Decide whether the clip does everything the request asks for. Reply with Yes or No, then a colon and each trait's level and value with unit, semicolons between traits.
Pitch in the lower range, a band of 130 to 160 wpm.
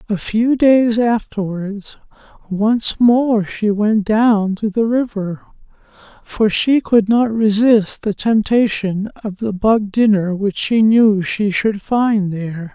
No: high, 210 Hz; average, 140 wpm